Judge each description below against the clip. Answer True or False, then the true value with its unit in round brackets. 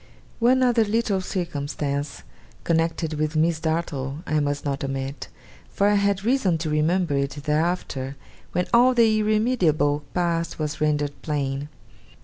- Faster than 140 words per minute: False (135 wpm)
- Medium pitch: True (160 Hz)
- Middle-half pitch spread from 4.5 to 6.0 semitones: True (5.4 semitones)